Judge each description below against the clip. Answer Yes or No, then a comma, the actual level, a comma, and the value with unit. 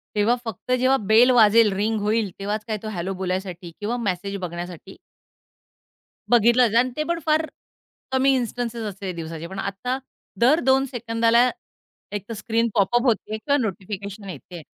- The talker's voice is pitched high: Yes, high, 220 Hz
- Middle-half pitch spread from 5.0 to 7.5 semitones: No, average, 3.8 semitones